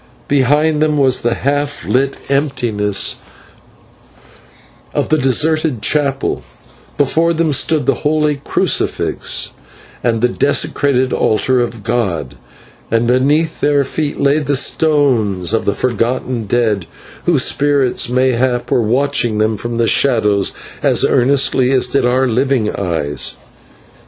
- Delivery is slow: Yes, slow, 125 wpm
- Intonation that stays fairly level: No, average, 3.7 semitones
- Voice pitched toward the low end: Yes, low, 130 Hz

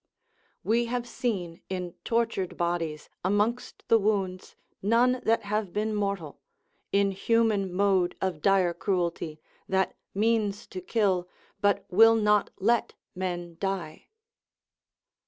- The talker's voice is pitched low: No, high, 200 Hz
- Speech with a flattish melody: No, average, 3.7 semitones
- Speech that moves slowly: Yes, slow, 115 wpm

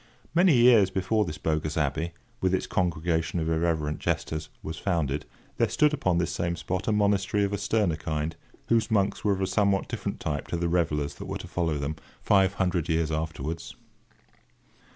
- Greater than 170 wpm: Yes, average, 185 wpm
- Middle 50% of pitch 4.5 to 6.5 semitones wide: No, average, 4.0 semitones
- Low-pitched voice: Yes, very low, 85 Hz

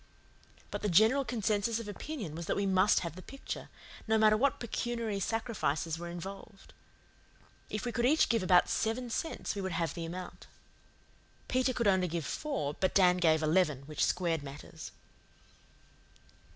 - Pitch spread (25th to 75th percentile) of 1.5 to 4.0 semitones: No, average, 5.2 semitones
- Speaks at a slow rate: No, average, 165 wpm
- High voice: Yes, high, 195 Hz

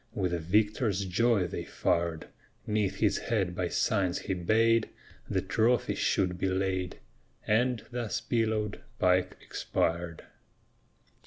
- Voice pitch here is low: Yes, very low, 95 Hz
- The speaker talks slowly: Yes, slow, 120 wpm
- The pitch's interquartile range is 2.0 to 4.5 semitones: Yes, average, 3.5 semitones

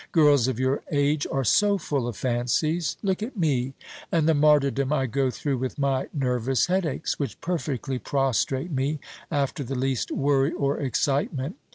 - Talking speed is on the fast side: No, average, 165 wpm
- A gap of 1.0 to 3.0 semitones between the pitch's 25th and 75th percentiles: Yes, average, 2.7 semitones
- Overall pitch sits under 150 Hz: Yes, medium, 140 Hz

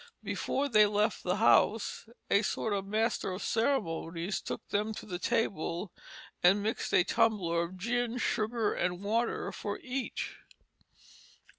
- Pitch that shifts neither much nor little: Yes, average, 3.7 semitones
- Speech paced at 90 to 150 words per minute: Yes, average, 140 wpm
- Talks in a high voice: Yes, high, 210 Hz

